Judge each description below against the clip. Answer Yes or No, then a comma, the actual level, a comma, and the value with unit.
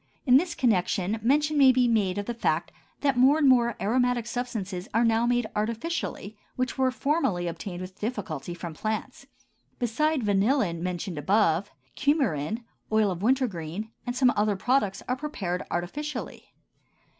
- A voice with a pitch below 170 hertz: No, high, 225 Hz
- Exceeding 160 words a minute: No, average, 150 wpm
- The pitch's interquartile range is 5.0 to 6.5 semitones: Yes, average, 5.3 semitones